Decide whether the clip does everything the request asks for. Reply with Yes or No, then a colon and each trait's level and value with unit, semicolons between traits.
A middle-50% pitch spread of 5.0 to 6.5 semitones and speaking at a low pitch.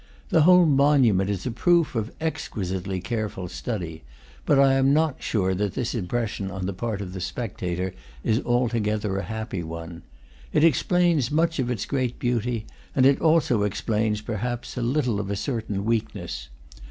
Yes: average, 5.3 semitones; low, 115 Hz